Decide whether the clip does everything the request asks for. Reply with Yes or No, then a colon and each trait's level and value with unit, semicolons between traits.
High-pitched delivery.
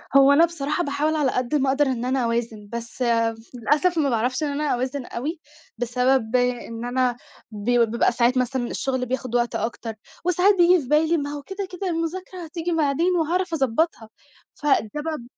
Yes: very high, 275 Hz